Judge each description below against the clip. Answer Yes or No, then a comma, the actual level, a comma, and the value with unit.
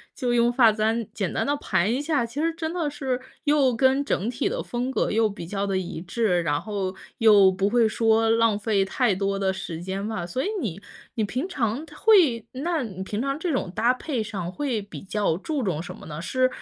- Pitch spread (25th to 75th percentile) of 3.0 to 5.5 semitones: Yes, average, 5.1 semitones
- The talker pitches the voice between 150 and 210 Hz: No, high, 225 Hz